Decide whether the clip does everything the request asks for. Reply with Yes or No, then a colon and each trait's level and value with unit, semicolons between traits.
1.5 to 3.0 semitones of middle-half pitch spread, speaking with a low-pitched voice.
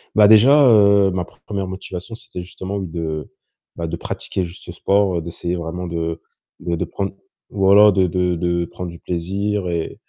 Yes: average, 2.7 semitones; very low, 90 Hz